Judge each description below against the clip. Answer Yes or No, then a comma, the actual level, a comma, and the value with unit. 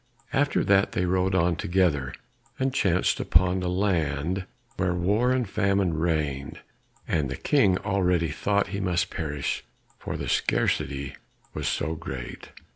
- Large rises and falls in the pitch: No, average, 3.7 semitones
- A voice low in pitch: Yes, very low, 90 Hz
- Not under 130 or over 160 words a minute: Yes, average, 140 wpm